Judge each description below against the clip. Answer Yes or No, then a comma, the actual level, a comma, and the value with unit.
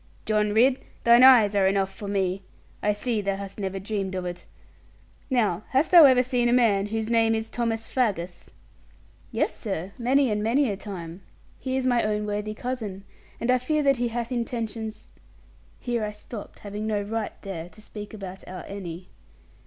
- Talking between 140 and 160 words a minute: No, average, 185 wpm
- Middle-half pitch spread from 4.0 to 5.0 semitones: No, average, 3.4 semitones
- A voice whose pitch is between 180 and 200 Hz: No, high, 215 Hz